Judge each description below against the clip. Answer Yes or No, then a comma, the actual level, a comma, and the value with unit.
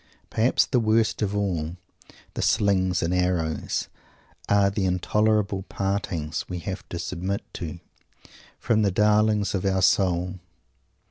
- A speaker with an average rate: No, slow, 130 wpm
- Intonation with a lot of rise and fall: No, narrow, 2.6 semitones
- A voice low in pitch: Yes, very low, 95 Hz